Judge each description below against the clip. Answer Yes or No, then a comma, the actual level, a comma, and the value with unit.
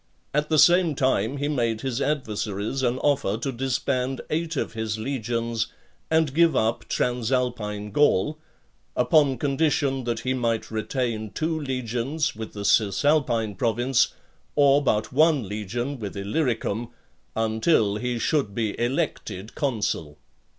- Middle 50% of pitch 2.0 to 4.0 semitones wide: No, average, 4.4 semitones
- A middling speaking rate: No, slow, 130 wpm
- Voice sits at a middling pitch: No, low, 125 Hz